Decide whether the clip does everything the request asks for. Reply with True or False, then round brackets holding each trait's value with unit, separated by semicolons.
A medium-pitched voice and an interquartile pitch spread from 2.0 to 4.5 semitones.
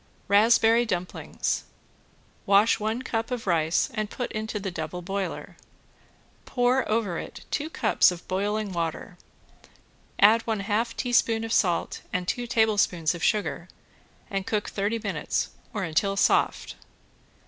False (210 Hz; 3.7 semitones)